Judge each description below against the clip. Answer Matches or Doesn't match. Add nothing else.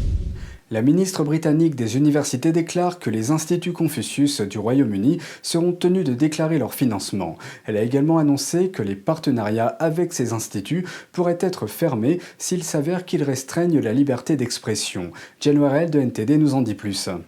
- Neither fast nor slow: Matches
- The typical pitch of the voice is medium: Matches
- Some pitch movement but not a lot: Doesn't match